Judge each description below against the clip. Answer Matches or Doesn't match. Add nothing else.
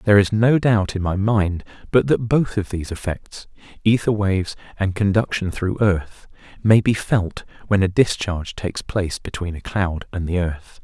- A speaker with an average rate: Matches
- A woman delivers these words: Doesn't match